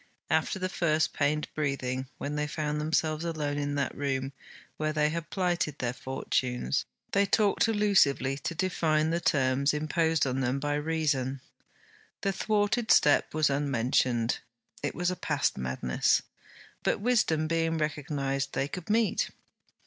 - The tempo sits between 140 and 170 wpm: Yes, average, 145 wpm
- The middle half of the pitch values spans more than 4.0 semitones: No, average, 3.4 semitones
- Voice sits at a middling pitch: Yes, medium, 150 Hz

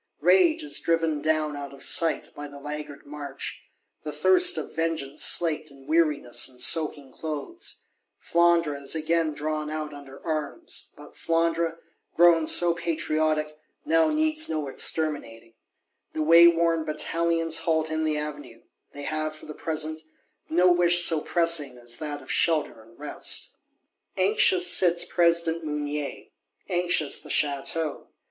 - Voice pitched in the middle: Yes, medium, 155 Hz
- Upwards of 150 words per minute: No, average, 140 wpm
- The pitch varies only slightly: Yes, narrow, 2.3 semitones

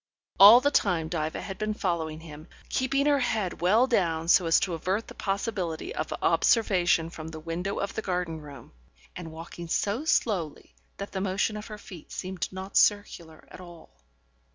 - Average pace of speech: Yes, average, 175 wpm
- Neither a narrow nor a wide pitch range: Yes, average, 4.2 semitones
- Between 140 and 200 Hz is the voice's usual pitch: Yes, medium, 185 Hz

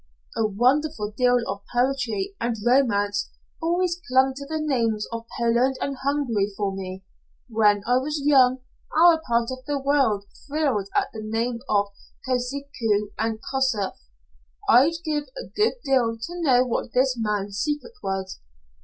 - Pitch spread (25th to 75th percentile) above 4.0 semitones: Yes, average, 4.6 semitones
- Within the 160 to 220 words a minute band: No, average, 150 wpm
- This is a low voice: No, very high, 250 Hz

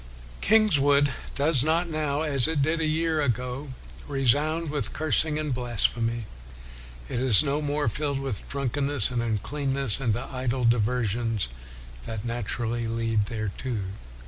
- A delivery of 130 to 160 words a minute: Yes, average, 140 wpm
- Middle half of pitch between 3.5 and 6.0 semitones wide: Yes, average, 4.1 semitones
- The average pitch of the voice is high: No, low, 135 Hz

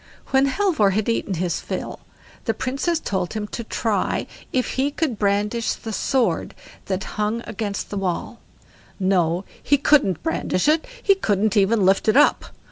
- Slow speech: No, average, 160 wpm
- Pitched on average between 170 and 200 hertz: No, high, 215 Hz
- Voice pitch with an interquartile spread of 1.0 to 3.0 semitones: No, wide, 5.4 semitones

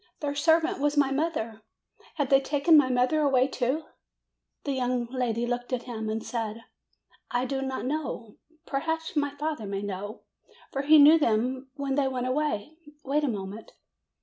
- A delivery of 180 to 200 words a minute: No, average, 170 wpm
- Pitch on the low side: No, very high, 265 Hz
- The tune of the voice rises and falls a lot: No, average, 3.5 semitones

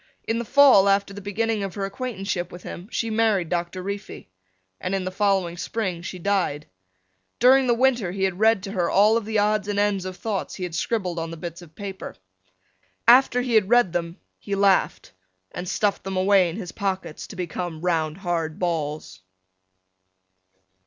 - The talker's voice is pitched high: Yes, high, 195 Hz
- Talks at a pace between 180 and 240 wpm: Yes, average, 185 wpm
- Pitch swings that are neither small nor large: Yes, average, 3.2 semitones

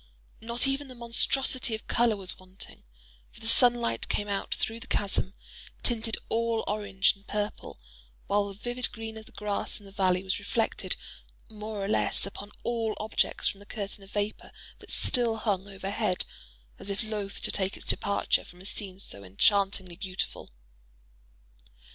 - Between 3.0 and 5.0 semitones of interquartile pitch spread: No, narrow, 2.4 semitones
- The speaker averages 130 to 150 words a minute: No, average, 170 wpm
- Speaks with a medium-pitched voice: No, high, 205 Hz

